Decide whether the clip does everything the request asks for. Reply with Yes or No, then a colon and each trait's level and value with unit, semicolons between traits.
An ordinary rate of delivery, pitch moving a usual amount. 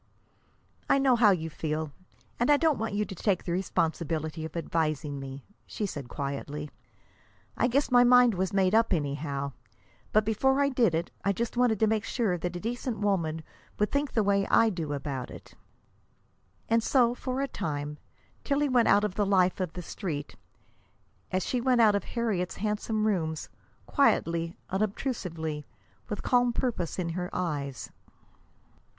No: average, 170 wpm; wide, 6.4 semitones